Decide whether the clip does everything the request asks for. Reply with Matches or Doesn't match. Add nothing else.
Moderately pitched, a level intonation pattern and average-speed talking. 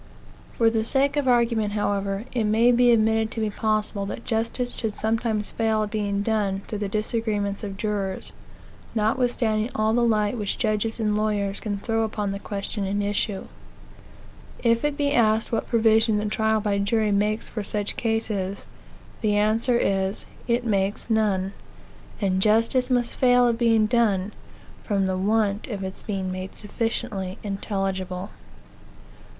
Doesn't match